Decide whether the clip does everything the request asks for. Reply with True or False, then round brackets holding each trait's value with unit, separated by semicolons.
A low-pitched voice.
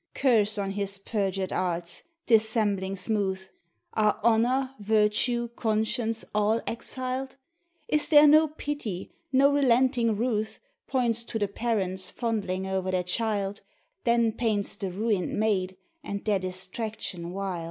False (215 Hz)